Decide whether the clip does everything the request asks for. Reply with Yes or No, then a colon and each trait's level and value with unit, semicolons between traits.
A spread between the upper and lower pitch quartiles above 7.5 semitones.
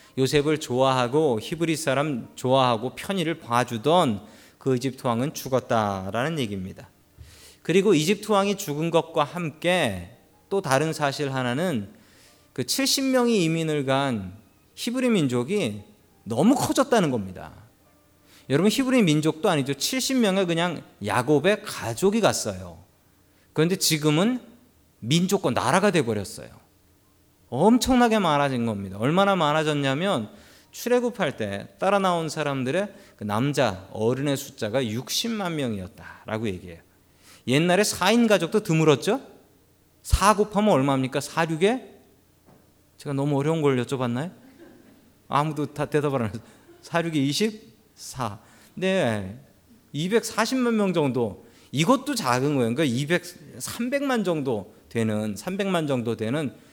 Yes: wide, 9.0 semitones